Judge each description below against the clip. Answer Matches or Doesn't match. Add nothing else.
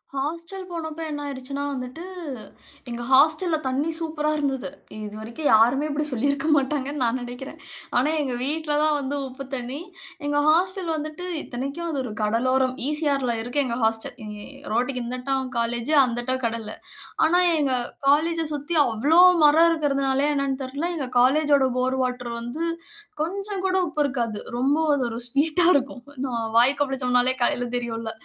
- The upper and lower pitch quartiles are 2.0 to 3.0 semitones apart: Doesn't match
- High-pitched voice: Matches